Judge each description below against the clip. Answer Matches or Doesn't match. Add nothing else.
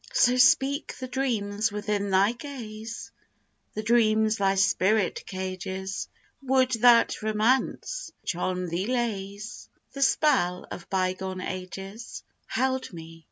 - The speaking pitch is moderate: Doesn't match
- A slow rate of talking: Matches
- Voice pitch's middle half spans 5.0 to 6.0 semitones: Doesn't match